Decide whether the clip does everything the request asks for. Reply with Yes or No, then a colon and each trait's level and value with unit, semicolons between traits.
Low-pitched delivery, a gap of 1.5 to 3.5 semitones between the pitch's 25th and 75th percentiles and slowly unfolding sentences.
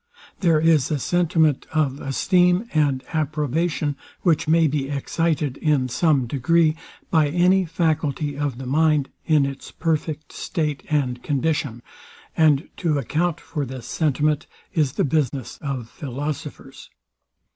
No: medium, 150 Hz; average, 2.7 semitones; slow, 130 wpm